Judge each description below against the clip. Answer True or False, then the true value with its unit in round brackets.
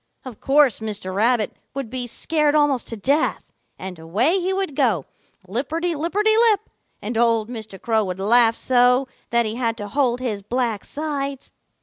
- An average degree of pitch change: True (4.9 semitones)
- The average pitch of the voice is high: True (245 Hz)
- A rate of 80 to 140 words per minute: False (165 wpm)